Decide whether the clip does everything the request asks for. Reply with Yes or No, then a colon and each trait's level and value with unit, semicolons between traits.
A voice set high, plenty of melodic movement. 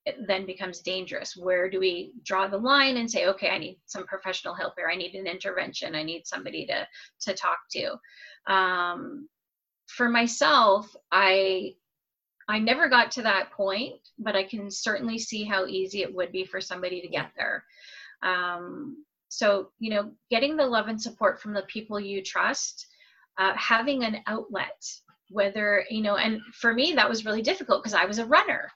No: high, 205 Hz; average, 4.0 semitones